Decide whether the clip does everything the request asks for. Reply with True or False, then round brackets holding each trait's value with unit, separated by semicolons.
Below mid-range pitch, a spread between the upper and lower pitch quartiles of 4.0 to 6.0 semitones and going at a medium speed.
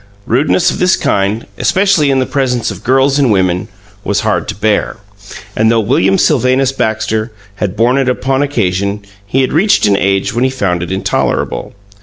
True (115 Hz; 5.0 semitones; 180 wpm)